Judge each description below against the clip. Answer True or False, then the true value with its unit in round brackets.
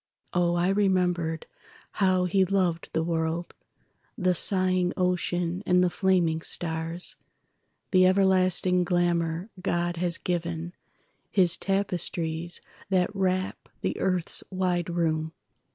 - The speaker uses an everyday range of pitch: False (1.5 semitones)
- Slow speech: True (105 wpm)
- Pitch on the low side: False (180 Hz)